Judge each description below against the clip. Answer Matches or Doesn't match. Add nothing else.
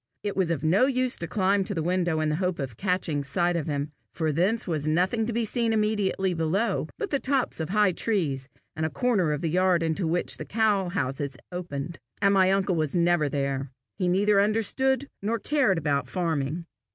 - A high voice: Doesn't match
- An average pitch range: Matches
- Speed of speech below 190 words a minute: Doesn't match